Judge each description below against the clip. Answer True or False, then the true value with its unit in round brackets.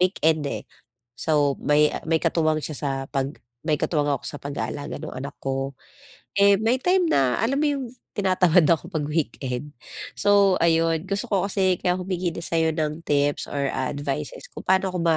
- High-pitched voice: False (160 Hz)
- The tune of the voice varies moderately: True (4.3 semitones)